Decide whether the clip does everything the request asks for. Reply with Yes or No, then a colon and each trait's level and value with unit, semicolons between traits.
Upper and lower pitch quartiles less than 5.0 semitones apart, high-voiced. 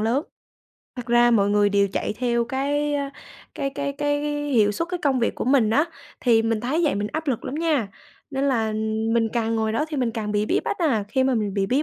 Yes: average, 4.4 semitones; high, 240 Hz